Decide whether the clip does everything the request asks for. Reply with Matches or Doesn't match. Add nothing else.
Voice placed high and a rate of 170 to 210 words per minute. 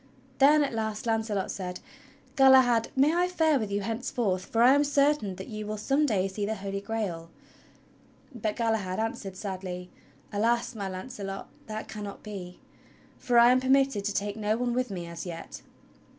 Matches